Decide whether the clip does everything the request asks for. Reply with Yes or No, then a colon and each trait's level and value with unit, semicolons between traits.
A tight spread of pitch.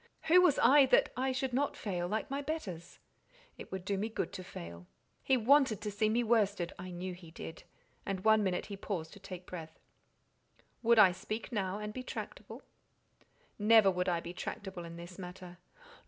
No: average, 4.5 semitones